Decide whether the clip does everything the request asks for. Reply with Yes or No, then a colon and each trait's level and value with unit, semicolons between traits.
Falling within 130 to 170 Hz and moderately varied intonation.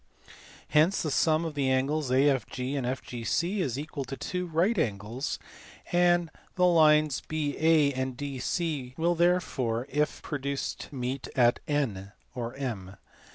Yes: medium, 140 Hz; average, 4.0 semitones